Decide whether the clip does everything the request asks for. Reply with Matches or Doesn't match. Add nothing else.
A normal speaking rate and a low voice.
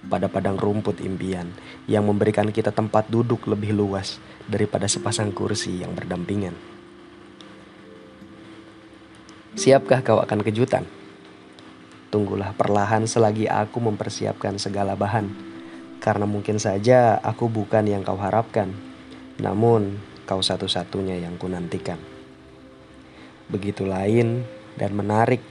Matches